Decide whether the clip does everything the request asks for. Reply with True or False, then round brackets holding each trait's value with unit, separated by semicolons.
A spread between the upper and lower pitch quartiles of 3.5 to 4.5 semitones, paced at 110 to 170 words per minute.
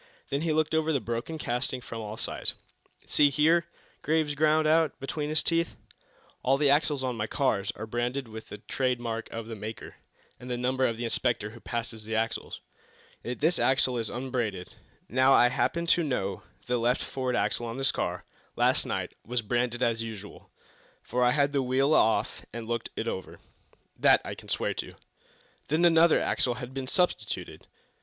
False (4.1 semitones; 190 wpm)